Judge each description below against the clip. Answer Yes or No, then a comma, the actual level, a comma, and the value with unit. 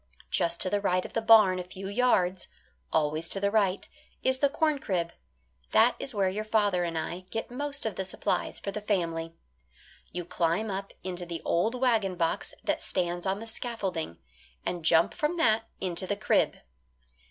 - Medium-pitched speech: No, high, 195 Hz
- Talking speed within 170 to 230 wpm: Yes, average, 185 wpm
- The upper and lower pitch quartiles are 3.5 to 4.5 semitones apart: Yes, average, 4.0 semitones